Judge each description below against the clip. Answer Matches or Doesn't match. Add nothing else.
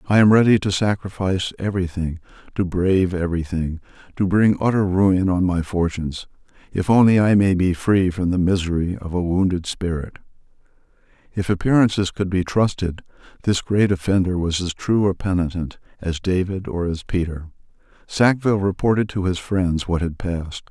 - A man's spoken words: Matches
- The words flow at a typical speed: Matches